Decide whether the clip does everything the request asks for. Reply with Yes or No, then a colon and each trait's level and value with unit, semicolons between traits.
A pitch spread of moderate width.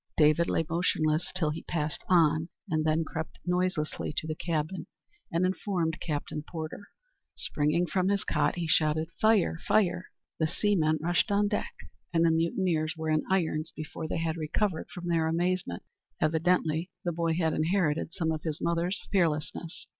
No: narrow, 2.3 semitones